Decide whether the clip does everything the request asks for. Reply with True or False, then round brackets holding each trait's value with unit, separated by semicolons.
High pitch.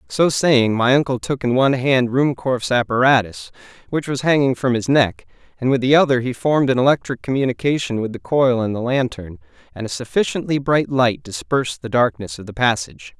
False (125 Hz)